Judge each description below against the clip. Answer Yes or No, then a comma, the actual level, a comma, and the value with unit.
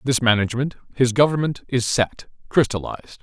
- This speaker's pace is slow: Yes, slow, 130 wpm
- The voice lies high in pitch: No, low, 125 Hz